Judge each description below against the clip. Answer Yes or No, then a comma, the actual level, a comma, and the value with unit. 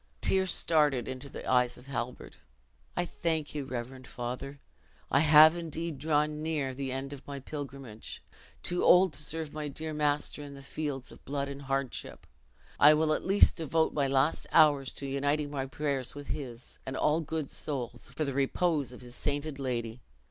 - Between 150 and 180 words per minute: Yes, average, 175 wpm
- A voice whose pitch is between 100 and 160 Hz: Yes, medium, 140 Hz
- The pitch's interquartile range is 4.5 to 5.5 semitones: No, narrow, 2.5 semitones